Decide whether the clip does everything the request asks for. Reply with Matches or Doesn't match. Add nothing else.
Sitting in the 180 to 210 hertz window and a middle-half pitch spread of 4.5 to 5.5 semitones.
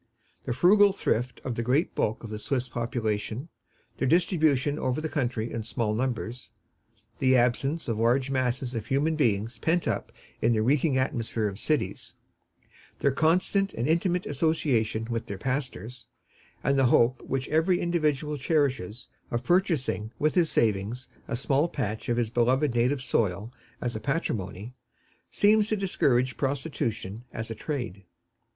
Doesn't match